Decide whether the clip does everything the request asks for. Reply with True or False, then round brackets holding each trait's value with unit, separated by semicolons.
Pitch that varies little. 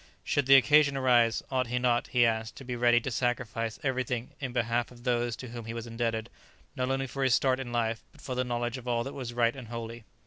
True (1.7 semitones)